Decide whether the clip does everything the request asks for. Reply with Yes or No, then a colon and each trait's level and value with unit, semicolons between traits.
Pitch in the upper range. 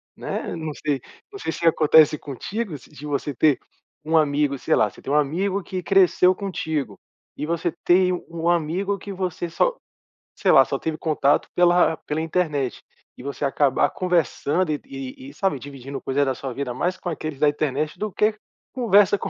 No: medium, 160 Hz